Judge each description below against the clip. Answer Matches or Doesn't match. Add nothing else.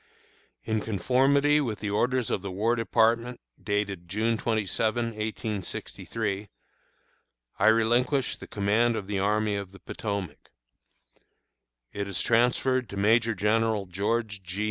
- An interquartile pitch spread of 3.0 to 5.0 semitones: Doesn't match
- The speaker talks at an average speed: Doesn't match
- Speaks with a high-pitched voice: Doesn't match